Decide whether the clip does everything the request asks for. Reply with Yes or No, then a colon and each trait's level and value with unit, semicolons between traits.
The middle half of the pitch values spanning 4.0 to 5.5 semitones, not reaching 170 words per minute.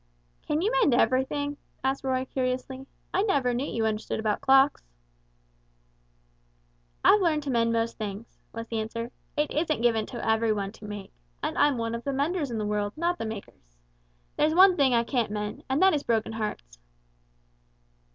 No: average, 4.6 semitones; average, 180 wpm